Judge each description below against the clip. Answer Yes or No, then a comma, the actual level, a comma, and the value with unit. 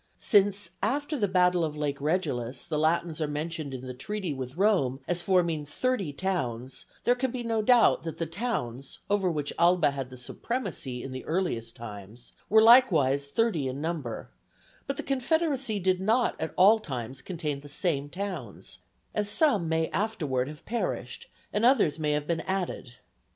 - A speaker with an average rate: Yes, average, 170 wpm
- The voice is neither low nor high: Yes, medium, 165 Hz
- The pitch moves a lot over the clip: Yes, wide, 6.8 semitones